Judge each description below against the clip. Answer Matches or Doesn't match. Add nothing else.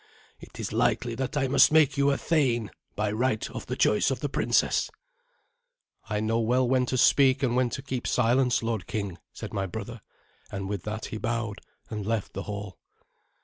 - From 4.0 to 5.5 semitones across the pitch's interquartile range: Doesn't match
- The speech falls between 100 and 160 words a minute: Doesn't match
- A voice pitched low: Matches